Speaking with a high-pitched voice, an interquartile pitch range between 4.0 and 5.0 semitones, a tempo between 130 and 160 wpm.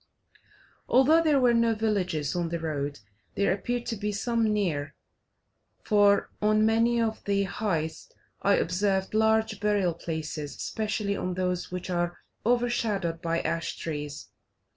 Yes: high, 200 Hz; average, 4.5 semitones; average, 140 wpm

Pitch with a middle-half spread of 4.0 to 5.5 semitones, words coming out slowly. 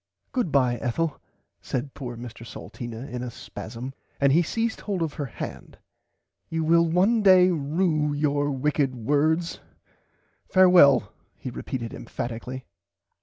Yes: average, 5.1 semitones; slow, 125 wpm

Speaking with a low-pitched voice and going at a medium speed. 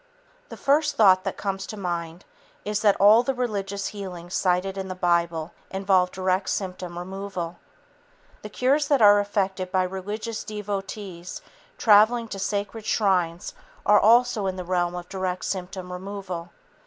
No: high, 195 Hz; average, 150 wpm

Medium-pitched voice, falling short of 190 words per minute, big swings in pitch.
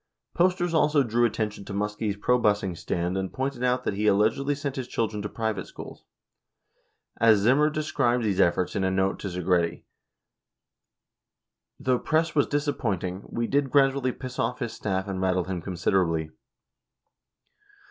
No: low, 110 Hz; average, 155 wpm; wide, 6.0 semitones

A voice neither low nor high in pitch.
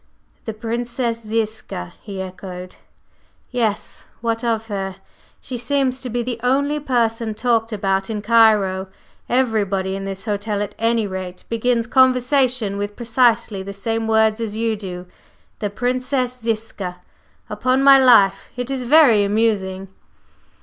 No: high, 225 Hz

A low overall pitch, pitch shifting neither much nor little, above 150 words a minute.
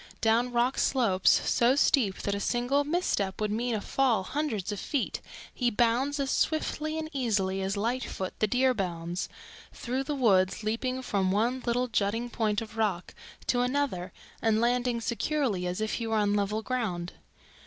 No: high, 230 Hz; average, 4.0 semitones; average, 170 wpm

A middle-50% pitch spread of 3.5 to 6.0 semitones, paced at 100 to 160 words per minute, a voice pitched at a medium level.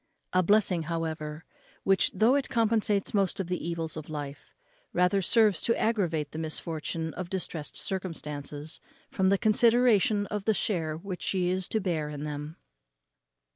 Yes: average, 4.4 semitones; average, 155 wpm; medium, 180 Hz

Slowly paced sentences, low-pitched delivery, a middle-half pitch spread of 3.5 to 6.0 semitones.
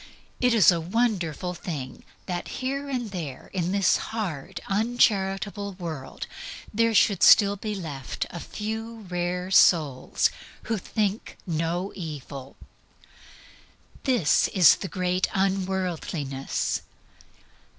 No: slow, 110 wpm; high, 190 Hz; average, 4.1 semitones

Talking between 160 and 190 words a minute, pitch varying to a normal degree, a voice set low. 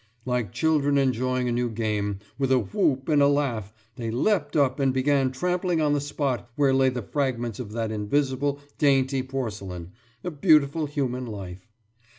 Yes: average, 170 wpm; average, 3.6 semitones; low, 130 Hz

